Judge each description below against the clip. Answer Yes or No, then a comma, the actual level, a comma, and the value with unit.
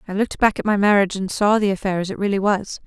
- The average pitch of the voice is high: Yes, high, 200 Hz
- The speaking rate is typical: No, fast, 295 wpm